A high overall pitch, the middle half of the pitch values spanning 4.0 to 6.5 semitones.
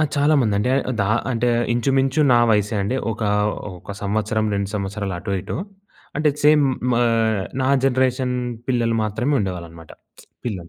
No: low, 115 Hz; average, 4.4 semitones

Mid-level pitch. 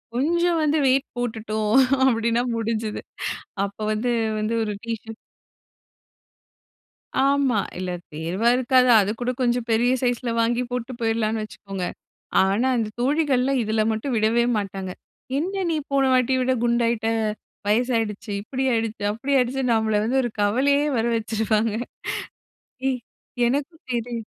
No: high, 235 Hz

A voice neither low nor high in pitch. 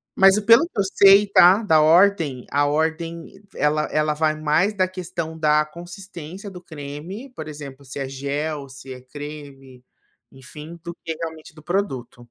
Yes: medium, 155 Hz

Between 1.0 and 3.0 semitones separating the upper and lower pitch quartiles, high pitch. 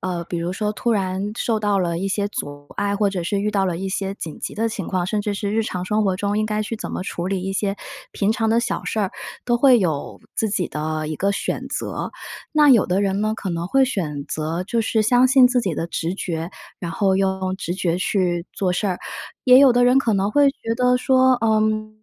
No: average, 3.4 semitones; high, 200 Hz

